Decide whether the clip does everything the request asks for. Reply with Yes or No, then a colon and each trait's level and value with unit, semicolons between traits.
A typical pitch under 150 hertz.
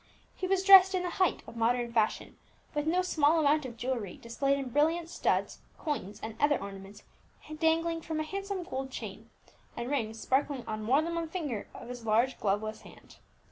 No: very high, 280 Hz